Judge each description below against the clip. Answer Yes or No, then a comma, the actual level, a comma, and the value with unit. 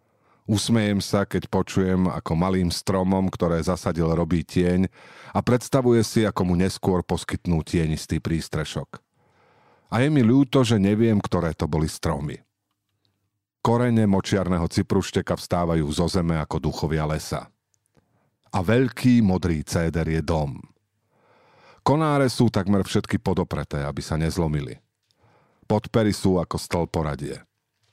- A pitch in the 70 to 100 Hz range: Yes, very low, 95 Hz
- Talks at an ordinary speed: Yes, average, 125 wpm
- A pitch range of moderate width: Yes, average, 4.0 semitones